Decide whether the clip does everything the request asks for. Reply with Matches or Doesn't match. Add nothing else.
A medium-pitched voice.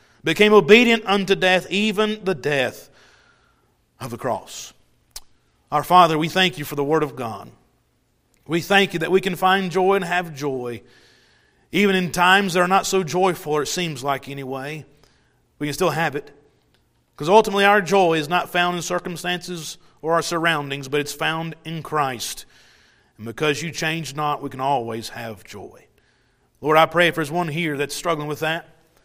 Matches